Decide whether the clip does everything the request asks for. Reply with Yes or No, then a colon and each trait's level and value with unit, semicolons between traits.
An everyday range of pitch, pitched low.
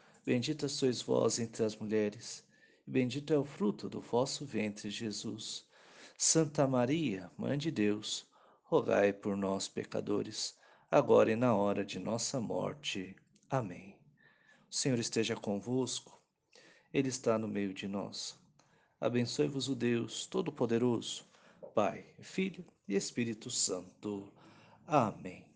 Yes: average, 4.4 semitones; low, 115 Hz